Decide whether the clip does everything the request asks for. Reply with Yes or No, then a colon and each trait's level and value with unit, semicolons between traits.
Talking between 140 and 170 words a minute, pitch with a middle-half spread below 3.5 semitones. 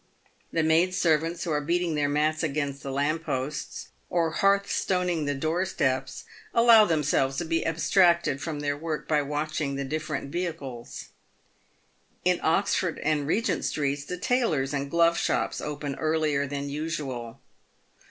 Yes: average, 150 wpm; average, 3.0 semitones